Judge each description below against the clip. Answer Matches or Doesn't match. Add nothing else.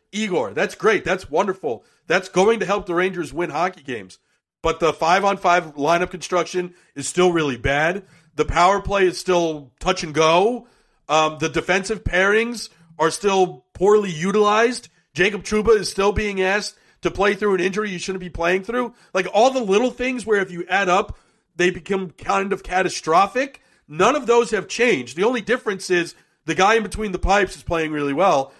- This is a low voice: Doesn't match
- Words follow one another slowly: Doesn't match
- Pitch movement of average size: Matches